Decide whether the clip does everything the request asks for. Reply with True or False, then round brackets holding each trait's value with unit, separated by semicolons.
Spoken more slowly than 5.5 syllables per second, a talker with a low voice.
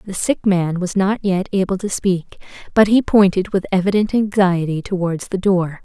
False (5.0 syllables/s; 190 Hz)